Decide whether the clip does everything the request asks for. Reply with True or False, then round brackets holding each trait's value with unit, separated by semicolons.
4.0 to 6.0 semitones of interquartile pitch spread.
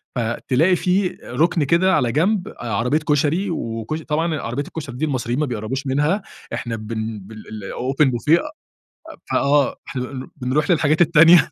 True (5.2 semitones)